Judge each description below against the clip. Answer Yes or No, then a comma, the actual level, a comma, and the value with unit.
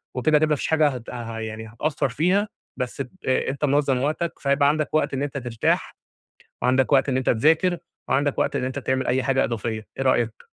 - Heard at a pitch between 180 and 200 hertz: No, low, 135 Hz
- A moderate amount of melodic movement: Yes, average, 3.1 semitones